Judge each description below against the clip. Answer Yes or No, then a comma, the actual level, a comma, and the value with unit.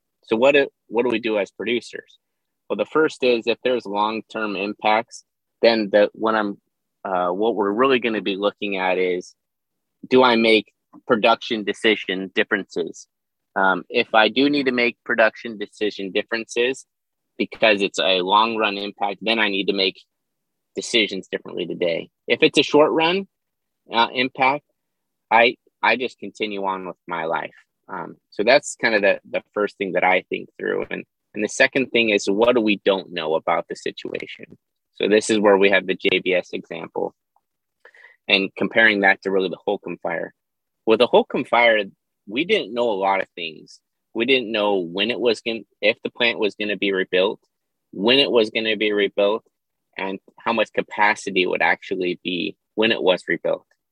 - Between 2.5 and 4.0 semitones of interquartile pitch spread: Yes, average, 3.3 semitones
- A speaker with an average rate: Yes, average, 180 wpm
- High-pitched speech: No, low, 105 Hz